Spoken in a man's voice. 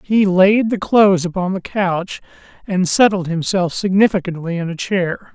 Yes: male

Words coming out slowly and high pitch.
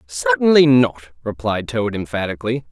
No: slow, 110 wpm; low, 110 Hz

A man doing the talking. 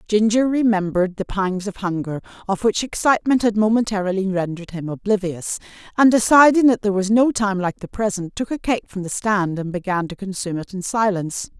No: female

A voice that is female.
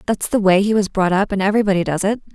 Yes: female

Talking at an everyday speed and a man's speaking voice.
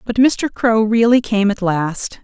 No: average, 190 wpm; female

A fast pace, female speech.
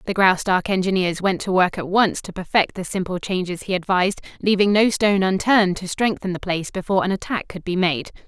Yes: fast, 210 wpm; female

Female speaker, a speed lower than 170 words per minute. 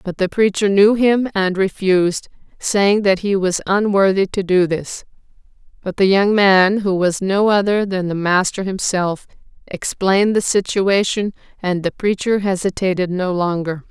Yes: female; average, 155 wpm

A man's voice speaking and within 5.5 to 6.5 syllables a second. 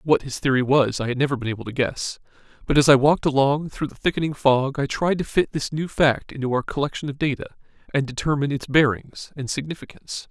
Yes: male; 6.1 syllables/s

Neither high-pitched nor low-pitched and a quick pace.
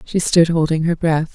Yes: medium, 165 Hz; fast, 225 wpm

